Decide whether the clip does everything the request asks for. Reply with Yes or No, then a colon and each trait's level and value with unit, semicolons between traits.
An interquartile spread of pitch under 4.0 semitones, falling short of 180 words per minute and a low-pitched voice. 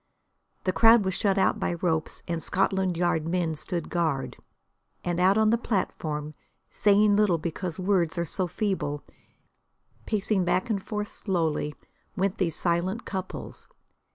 No: average, 3.0 semitones; average, 145 wpm; medium, 185 Hz